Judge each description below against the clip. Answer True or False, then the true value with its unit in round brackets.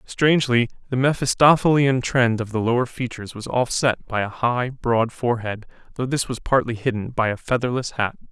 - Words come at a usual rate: True (175 wpm)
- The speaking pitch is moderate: False (120 Hz)